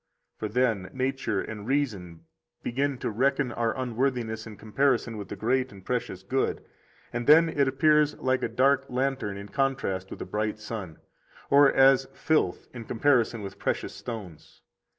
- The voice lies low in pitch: Yes, low, 120 Hz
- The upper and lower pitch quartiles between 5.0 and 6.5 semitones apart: No, average, 4.3 semitones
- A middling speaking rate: Yes, average, 165 wpm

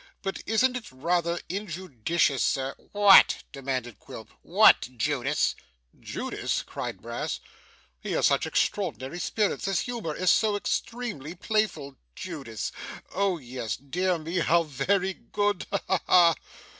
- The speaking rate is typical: No, slow, 130 wpm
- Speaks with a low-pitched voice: No, medium, 170 Hz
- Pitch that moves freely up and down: Yes, wide, 6.5 semitones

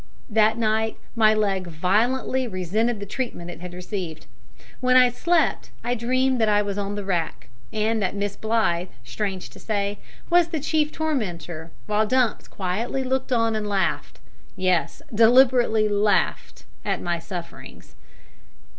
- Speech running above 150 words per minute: No, average, 145 wpm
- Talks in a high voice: Yes, high, 215 Hz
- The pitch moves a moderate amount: Yes, average, 4.4 semitones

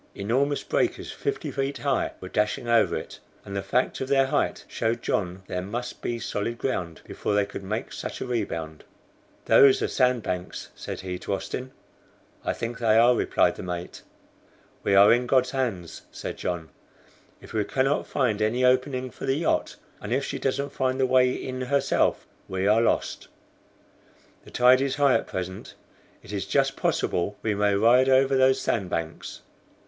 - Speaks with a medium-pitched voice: No, low, 120 Hz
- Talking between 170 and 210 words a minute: Yes, average, 180 wpm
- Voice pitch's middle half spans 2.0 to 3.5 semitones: No, average, 4.7 semitones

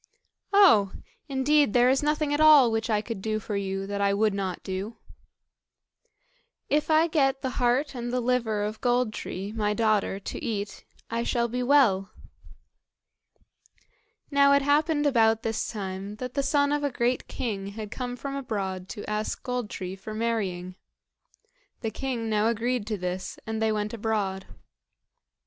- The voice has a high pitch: Yes, high, 225 Hz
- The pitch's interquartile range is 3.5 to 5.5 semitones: Yes, average, 4.1 semitones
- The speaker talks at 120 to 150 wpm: No, average, 165 wpm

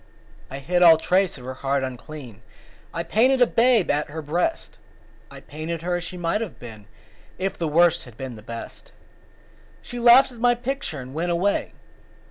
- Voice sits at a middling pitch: Yes, medium, 170 Hz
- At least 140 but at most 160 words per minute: No, average, 185 wpm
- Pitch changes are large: Yes, wide, 6.6 semitones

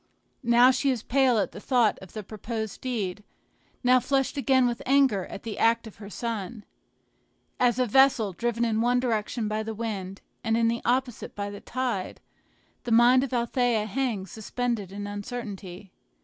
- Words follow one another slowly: No, average, 175 wpm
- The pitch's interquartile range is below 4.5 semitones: Yes, average, 3.1 semitones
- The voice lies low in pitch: No, high, 230 Hz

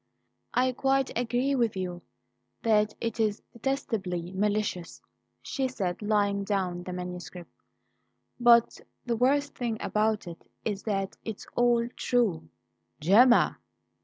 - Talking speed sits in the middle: No, slow, 120 wpm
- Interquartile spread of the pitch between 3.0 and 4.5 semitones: Yes, average, 4.2 semitones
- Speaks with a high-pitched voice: Yes, high, 215 Hz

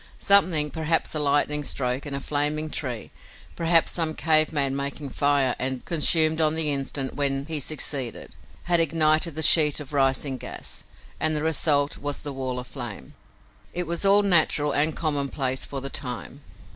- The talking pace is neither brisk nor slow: Yes, average, 170 wpm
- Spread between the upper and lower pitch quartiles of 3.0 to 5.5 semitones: No, narrow, 2.4 semitones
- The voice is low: No, medium, 150 Hz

